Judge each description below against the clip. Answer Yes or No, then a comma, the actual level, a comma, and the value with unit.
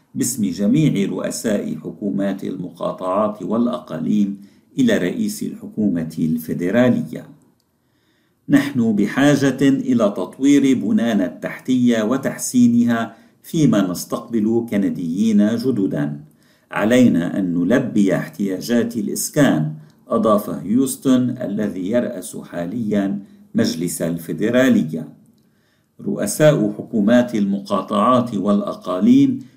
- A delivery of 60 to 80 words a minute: Yes, average, 75 wpm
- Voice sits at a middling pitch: No, low, 120 Hz